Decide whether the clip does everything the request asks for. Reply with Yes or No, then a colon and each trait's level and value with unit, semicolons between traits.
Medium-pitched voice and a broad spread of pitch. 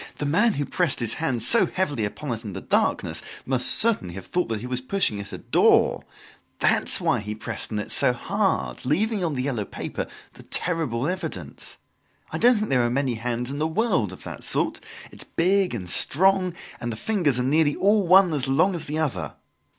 Yes: medium, 145 Hz; wide, 7.4 semitones